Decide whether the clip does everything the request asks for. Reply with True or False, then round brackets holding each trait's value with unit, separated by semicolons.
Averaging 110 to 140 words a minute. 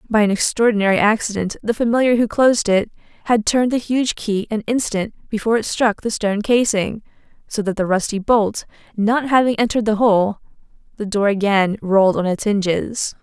False (175 wpm)